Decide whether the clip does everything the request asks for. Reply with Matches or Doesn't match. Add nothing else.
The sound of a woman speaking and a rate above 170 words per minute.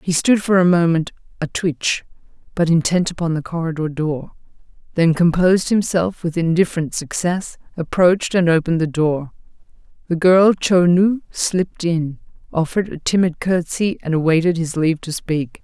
Doesn't match